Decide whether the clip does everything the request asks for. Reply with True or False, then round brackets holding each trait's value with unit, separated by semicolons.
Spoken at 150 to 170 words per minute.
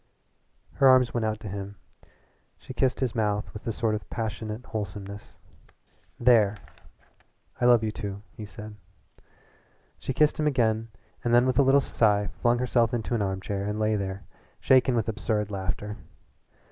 True (160 wpm)